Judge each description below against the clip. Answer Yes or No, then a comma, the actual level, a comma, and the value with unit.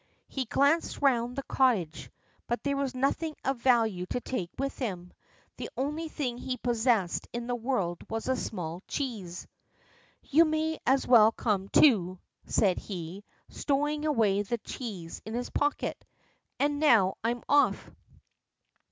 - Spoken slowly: No, average, 145 wpm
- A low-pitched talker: No, high, 245 Hz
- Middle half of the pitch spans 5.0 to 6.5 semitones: Yes, wide, 5.4 semitones